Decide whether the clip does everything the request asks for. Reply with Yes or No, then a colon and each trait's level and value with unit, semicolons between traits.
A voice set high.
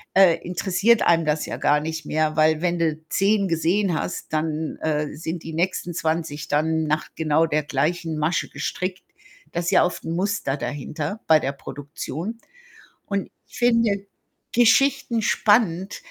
No: medium, 165 Hz